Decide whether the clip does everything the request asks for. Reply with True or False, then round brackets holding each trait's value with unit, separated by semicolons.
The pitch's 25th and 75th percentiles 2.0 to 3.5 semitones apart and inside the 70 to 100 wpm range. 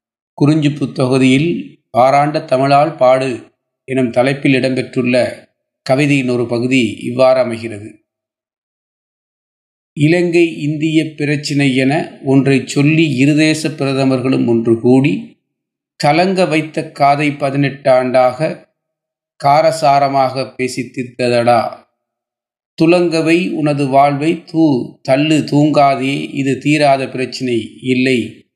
True (3.2 semitones; 90 wpm)